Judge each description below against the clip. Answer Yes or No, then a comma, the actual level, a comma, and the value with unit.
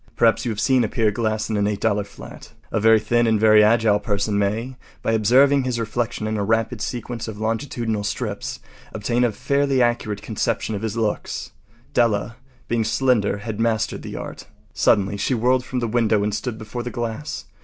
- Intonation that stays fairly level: Yes, narrow, 2.2 semitones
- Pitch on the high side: No, low, 110 Hz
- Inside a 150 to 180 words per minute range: No, average, 190 wpm